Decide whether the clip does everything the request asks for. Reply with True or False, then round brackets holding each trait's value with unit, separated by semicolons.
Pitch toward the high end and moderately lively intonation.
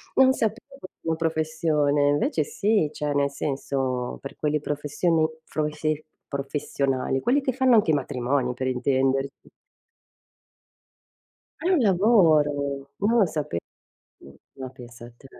False (150 Hz; 3.4 semitones)